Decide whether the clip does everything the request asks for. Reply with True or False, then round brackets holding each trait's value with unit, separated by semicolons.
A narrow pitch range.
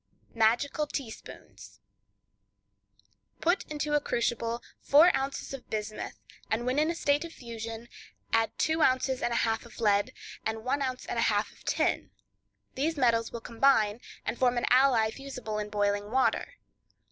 False (3.7 semitones)